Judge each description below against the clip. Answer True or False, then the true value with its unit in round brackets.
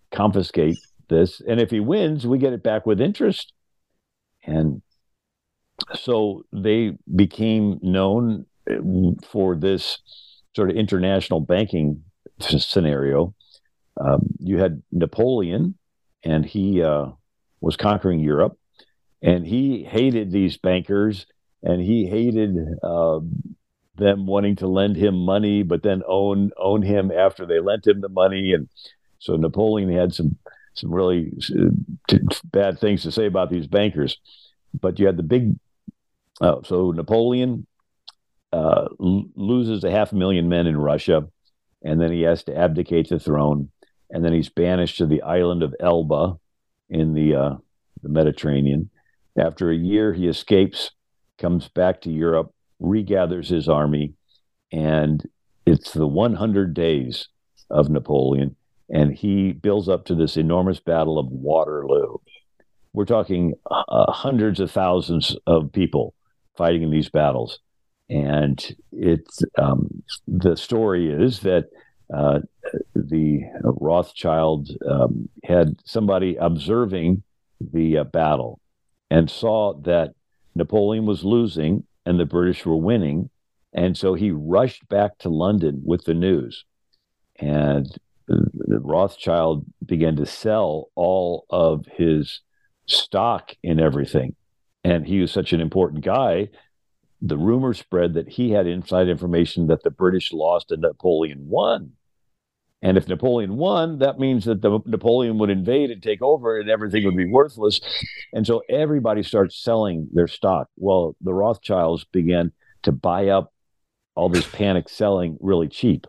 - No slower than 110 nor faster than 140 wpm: True (135 wpm)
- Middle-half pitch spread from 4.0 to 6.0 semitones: True (4.4 semitones)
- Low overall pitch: True (90 Hz)